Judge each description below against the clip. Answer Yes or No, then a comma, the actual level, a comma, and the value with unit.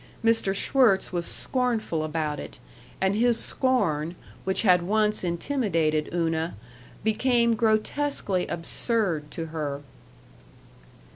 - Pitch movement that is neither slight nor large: No, wide, 5.9 semitones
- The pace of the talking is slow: Yes, slow, 100 wpm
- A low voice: No, high, 190 Hz